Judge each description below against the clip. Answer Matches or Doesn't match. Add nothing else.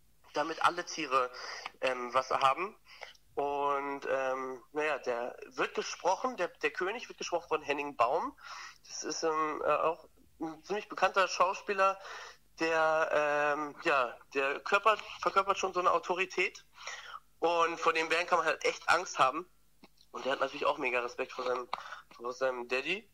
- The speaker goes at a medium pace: Matches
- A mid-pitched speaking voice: Matches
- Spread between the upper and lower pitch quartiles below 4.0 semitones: Doesn't match